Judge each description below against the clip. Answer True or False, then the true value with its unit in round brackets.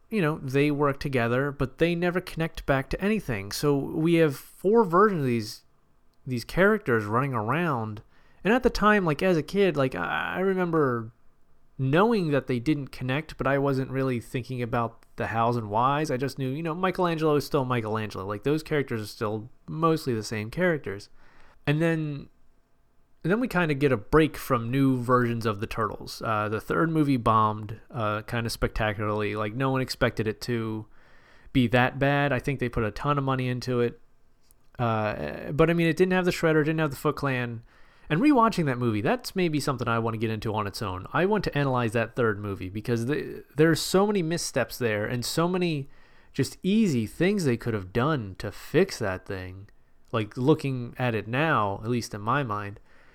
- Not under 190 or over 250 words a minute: True (200 wpm)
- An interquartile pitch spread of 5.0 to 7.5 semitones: True (5.6 semitones)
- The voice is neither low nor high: False (130 Hz)